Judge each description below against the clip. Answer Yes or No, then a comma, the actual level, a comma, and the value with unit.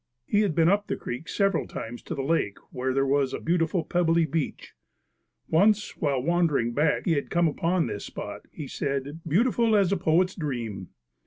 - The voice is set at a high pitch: No, medium, 160 Hz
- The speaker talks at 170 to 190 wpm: Yes, average, 185 wpm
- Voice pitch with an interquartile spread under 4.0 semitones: No, average, 4.6 semitones